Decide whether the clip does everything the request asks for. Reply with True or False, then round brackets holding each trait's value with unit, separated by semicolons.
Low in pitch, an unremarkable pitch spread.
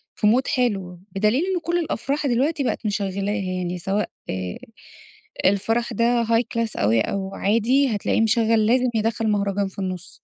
False (220 Hz; 3.6 semitones)